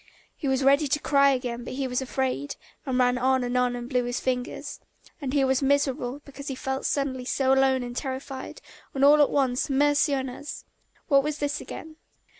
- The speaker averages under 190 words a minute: No, fast, 205 wpm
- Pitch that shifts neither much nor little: No, narrow, 1.9 semitones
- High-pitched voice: Yes, very high, 265 Hz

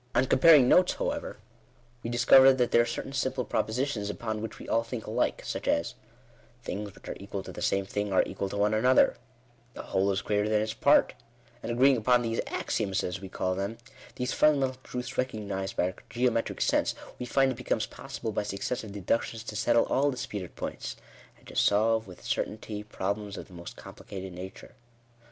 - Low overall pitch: Yes, low, 110 Hz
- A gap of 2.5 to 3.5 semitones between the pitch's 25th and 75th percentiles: No, average, 3.9 semitones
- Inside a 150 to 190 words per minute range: No, average, 200 wpm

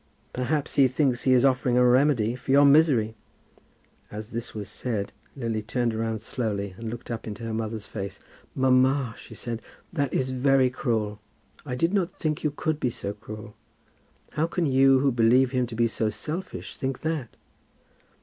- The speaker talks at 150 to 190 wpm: Yes, average, 180 wpm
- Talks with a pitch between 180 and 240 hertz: No, low, 125 Hz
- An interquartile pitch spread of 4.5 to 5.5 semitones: No, average, 3.5 semitones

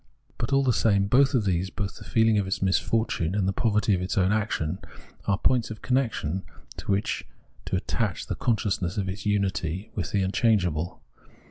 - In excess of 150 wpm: Yes, average, 190 wpm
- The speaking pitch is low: Yes, low, 100 Hz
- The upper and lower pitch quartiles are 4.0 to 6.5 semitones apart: No, average, 3.0 semitones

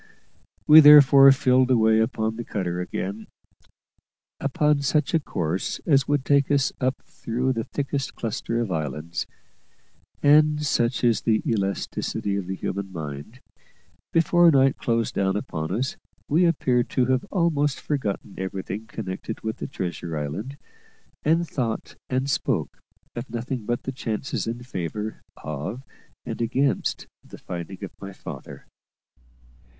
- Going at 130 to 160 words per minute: Yes, average, 140 wpm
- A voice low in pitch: Yes, low, 120 Hz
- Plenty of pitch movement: Yes, wide, 5.8 semitones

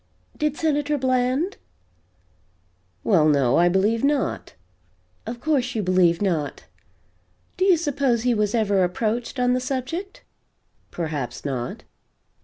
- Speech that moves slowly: Yes, slow, 120 wpm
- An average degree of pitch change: No, wide, 7.3 semitones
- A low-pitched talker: No, high, 235 Hz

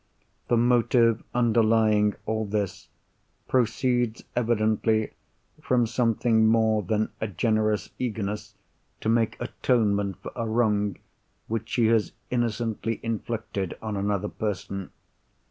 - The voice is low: Yes, low, 110 Hz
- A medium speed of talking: No, slow, 110 wpm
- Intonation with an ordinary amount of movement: No, narrow, 1.9 semitones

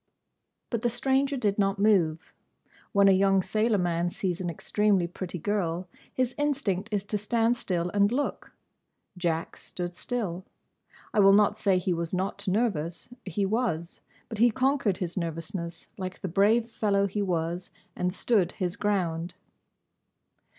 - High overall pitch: Yes, high, 195 Hz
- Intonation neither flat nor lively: Yes, average, 3.4 semitones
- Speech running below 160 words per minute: Yes, average, 150 wpm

